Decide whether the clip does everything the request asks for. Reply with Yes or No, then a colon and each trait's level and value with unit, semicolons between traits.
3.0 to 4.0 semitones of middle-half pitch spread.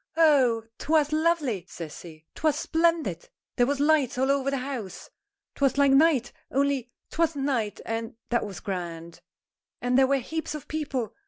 No: average, 4.9 semitones